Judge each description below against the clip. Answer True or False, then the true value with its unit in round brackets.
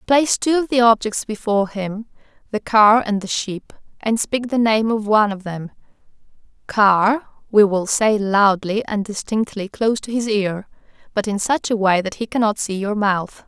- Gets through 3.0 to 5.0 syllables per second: True (4.7 syllables/s)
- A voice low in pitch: False (215 Hz)